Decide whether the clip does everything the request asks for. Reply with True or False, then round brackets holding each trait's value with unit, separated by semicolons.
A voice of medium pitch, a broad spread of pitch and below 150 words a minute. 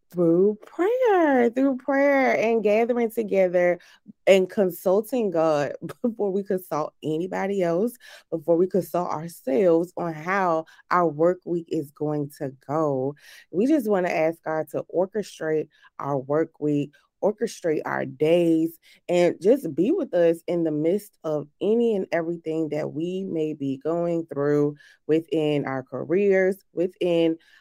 False (170 Hz; 4.1 semitones; 140 wpm)